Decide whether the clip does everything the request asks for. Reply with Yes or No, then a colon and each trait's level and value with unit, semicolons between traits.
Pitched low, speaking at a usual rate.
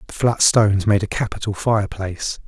Yes: low, 105 Hz; average, 170 wpm